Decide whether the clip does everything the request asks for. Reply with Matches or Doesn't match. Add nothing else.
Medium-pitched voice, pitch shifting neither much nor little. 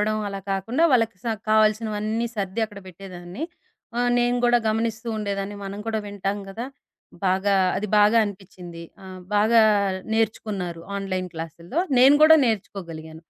Doesn't match